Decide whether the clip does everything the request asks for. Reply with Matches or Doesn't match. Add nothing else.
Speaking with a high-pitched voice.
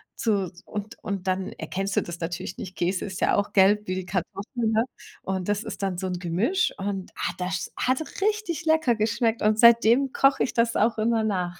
Matches